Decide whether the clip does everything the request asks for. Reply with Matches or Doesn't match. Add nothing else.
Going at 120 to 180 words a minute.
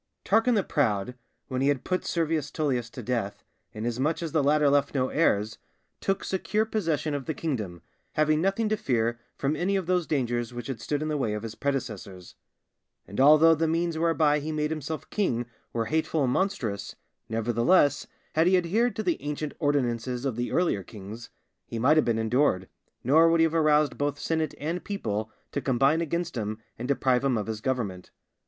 Doesn't match